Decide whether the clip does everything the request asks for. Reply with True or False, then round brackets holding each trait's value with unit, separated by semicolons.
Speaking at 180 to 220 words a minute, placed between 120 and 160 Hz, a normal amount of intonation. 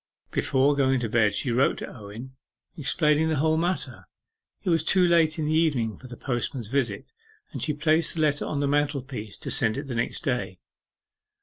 True (195 wpm; 140 Hz; 4.3 semitones)